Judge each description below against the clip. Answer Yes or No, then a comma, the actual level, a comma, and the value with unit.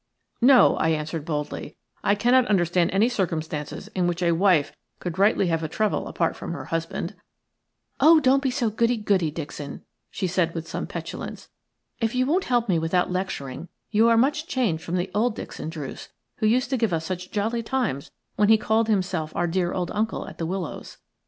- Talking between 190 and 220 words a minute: Yes, average, 195 wpm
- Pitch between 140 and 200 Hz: Yes, high, 190 Hz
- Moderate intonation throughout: No, wide, 5.7 semitones